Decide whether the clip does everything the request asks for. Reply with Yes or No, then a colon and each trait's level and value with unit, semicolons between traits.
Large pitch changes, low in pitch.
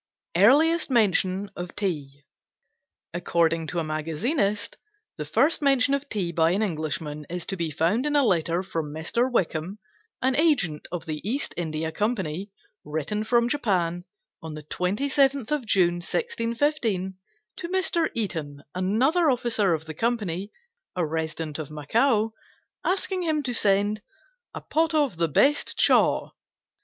No: wide, 7.7 semitones; high, 195 Hz